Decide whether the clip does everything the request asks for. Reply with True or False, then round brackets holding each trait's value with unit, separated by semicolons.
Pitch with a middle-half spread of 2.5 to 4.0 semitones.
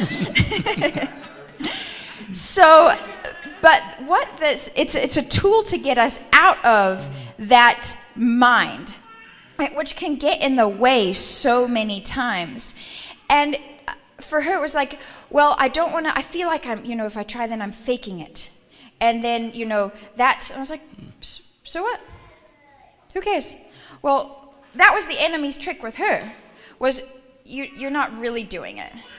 False (4.9 semitones)